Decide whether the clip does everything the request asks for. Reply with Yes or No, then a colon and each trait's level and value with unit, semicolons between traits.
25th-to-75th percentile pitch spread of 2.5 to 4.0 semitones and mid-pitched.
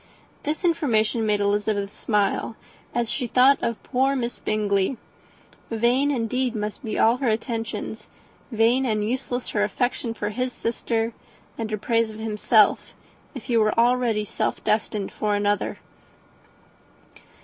No: average, 2.8 semitones; high, 225 Hz